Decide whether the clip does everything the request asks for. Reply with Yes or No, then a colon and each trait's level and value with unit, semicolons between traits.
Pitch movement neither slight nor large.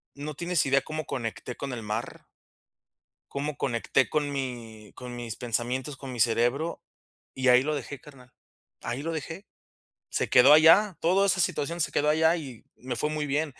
Yes: average, 3.8 semitones